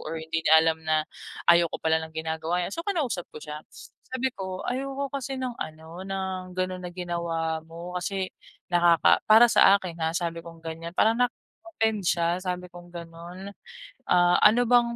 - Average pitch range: Yes, average, 3.3 semitones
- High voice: No, medium, 175 Hz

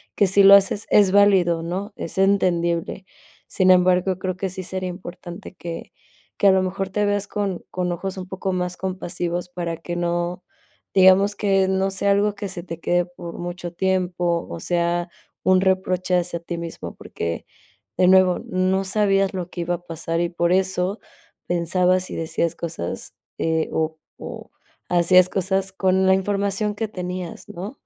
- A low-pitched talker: No, medium, 185 Hz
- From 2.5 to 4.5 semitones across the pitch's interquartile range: No, narrow, 1.7 semitones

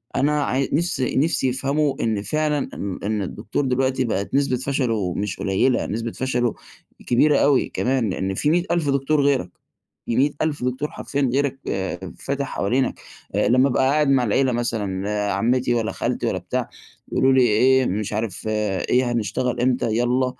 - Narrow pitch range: No, average, 3.5 semitones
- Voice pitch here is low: Yes, low, 130 Hz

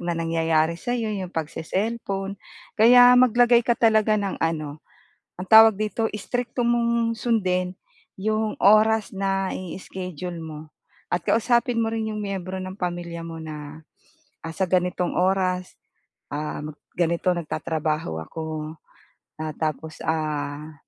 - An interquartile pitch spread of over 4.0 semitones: Yes, average, 5.2 semitones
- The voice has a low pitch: No, medium, 185 Hz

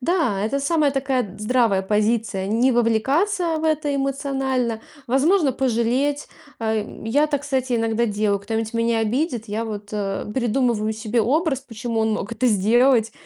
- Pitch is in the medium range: No, high, 235 Hz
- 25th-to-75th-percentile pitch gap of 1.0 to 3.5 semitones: No, average, 3.9 semitones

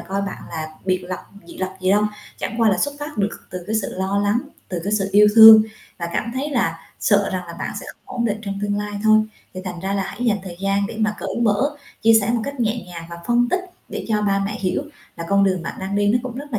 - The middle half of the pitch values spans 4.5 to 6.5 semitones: No, average, 2.9 semitones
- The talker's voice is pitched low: No, high, 205 Hz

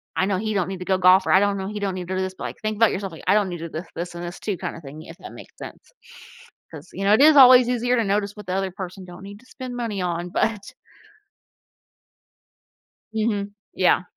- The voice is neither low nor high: No, high, 195 Hz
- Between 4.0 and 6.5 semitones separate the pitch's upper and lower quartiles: No, average, 2.7 semitones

